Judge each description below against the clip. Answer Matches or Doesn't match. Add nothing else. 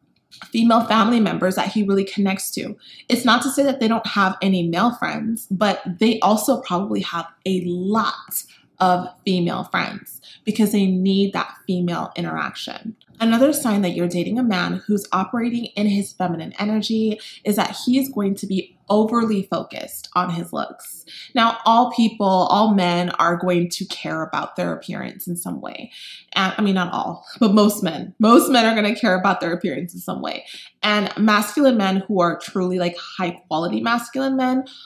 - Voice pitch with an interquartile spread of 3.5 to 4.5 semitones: Matches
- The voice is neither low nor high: Doesn't match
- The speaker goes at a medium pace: Matches